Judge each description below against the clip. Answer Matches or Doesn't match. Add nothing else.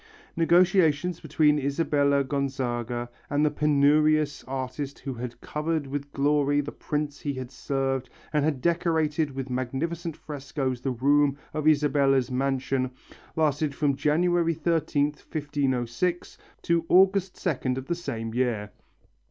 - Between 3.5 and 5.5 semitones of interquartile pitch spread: Doesn't match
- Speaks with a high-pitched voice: Doesn't match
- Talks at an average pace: Doesn't match